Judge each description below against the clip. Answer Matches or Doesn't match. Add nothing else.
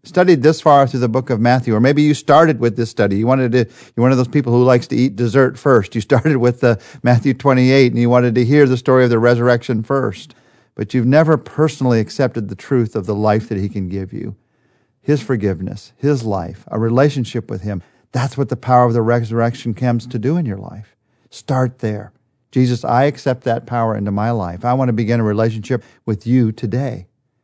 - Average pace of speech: Doesn't match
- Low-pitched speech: Matches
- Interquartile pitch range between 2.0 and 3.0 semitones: Matches